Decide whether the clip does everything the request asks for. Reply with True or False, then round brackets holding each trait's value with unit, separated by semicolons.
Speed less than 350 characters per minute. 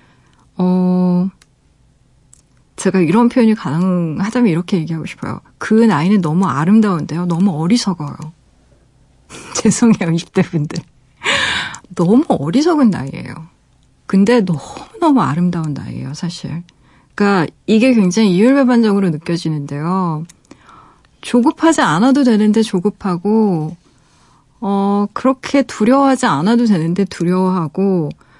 True (275 characters per minute)